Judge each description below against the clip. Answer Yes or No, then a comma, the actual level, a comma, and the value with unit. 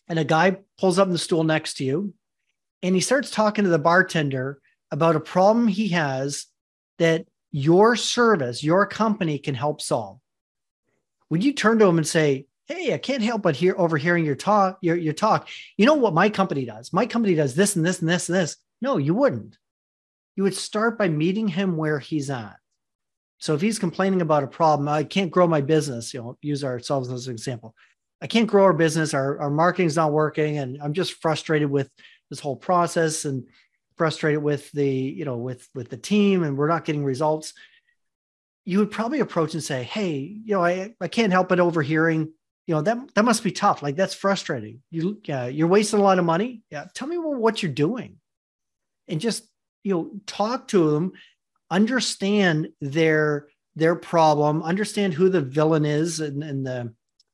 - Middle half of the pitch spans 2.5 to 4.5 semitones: No, average, 4.9 semitones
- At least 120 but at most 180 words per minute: No, average, 200 wpm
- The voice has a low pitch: No, medium, 165 Hz